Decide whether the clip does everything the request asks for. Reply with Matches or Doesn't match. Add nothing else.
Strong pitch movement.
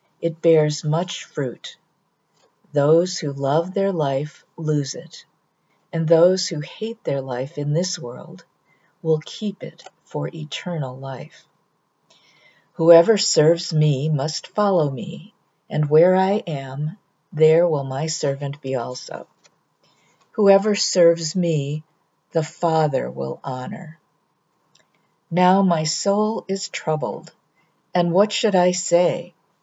Doesn't match